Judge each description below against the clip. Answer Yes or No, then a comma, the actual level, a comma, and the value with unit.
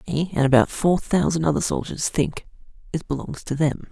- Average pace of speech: Yes, average, 185 wpm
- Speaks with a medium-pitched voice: Yes, medium, 145 Hz